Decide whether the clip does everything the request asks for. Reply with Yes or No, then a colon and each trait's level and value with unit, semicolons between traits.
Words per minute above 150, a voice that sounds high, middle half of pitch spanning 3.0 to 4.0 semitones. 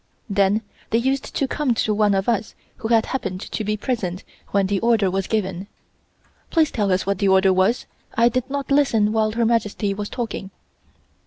Yes: average, 190 wpm; high, 215 Hz; average, 3.3 semitones